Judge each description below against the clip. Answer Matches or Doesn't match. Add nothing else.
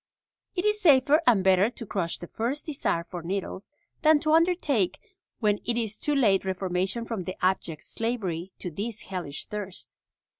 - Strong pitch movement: Matches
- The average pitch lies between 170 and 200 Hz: Doesn't match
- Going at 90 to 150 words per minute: Doesn't match